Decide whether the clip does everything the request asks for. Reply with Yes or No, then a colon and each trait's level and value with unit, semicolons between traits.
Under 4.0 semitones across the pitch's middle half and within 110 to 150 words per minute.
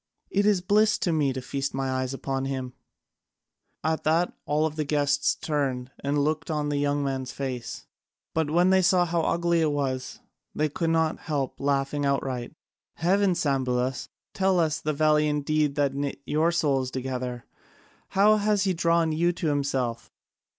No: average, 3.5 semitones; average, 165 wpm